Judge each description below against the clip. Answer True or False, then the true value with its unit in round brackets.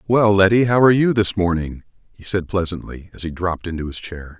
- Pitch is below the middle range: True (95 Hz)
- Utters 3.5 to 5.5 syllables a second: False (5.9 syllables/s)